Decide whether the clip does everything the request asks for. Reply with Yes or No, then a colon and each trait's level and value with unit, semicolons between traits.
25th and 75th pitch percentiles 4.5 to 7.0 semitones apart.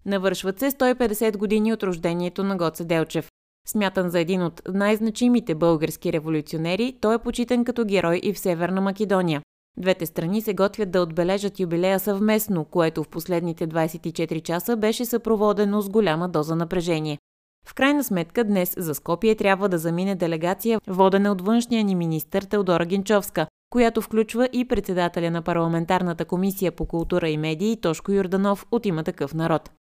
No: average, 4.0 semitones